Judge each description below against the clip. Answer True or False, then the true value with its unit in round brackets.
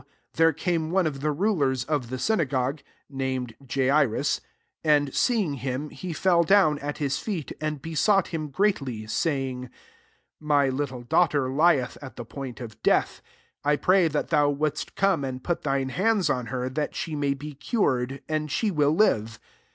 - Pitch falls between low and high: True (145 Hz)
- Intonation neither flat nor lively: True (3.6 semitones)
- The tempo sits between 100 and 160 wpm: False (175 wpm)